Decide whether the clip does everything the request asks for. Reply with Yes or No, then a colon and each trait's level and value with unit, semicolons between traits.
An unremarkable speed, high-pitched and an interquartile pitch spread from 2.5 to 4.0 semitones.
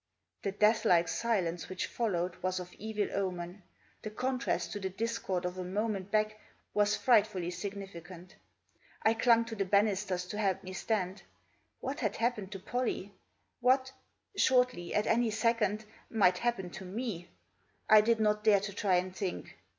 Yes: average, 165 wpm; high, 205 Hz; average, 3.3 semitones